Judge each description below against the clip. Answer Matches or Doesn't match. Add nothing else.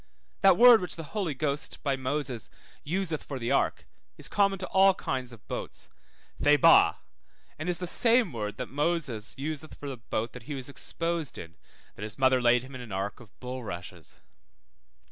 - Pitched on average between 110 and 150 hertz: Matches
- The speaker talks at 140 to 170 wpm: Doesn't match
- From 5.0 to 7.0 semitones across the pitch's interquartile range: Matches